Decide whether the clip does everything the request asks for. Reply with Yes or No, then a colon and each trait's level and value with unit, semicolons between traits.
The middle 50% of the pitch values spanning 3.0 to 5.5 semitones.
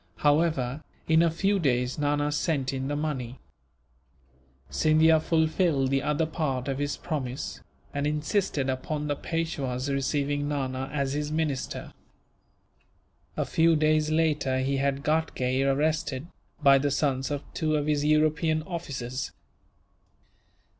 No: narrow, 2.5 semitones